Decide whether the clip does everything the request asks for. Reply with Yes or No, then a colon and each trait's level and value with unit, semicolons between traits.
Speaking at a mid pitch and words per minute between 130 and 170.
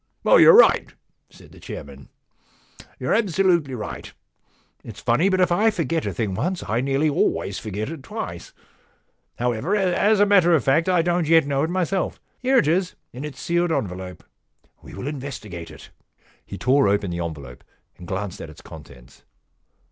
No: medium, 145 Hz; average, 180 wpm